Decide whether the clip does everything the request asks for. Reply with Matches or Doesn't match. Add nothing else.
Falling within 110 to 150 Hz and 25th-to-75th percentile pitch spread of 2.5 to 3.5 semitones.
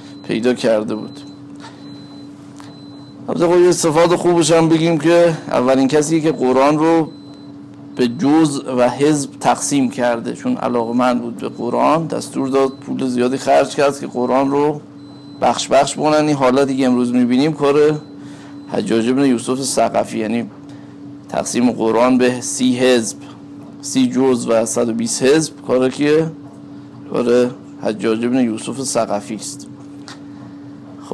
Matches